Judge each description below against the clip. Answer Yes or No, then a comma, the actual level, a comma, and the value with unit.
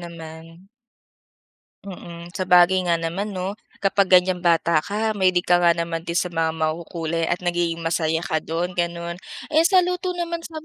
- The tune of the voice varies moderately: No, narrow, 2.2 semitones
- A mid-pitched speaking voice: Yes, medium, 175 Hz